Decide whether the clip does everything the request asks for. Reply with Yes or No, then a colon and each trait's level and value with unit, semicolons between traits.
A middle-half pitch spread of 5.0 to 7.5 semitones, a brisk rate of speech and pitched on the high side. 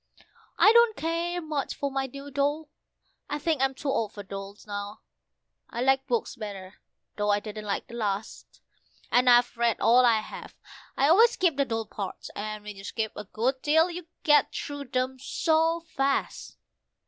No: wide, 5.6 semitones; average, 180 wpm; very high, 260 Hz